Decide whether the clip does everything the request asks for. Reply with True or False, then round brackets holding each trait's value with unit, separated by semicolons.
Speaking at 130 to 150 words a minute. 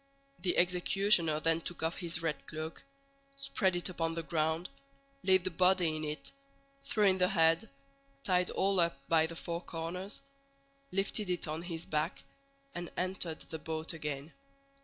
False (160 wpm)